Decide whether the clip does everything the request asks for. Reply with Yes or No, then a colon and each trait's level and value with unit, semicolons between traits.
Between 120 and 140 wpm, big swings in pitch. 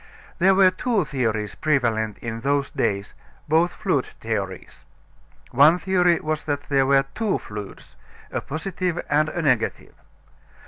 Yes: slow, 135 wpm; wide, 7.4 semitones